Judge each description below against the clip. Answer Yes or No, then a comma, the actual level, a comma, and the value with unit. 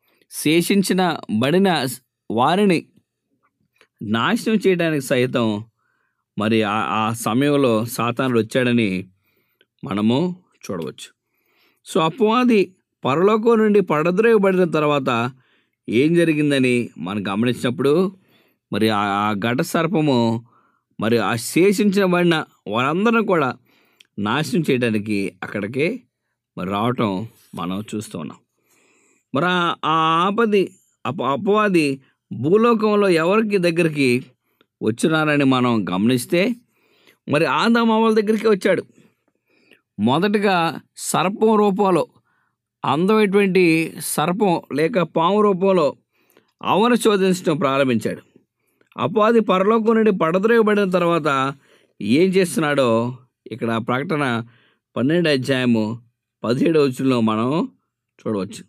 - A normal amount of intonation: No, wide, 8.4 semitones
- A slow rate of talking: Yes, slow, 80 wpm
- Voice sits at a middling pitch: Yes, medium, 155 Hz